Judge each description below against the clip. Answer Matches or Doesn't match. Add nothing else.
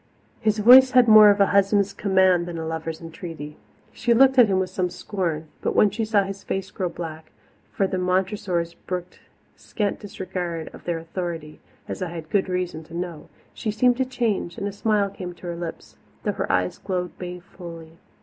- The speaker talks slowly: Doesn't match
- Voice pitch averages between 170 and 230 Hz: Matches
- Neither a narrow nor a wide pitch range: Matches